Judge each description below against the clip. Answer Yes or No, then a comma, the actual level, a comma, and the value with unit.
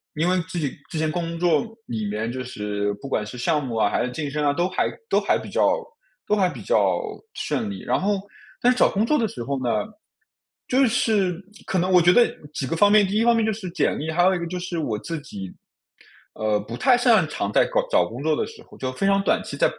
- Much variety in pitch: Yes, wide, 8.2 semitones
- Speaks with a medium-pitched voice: Yes, medium, 170 Hz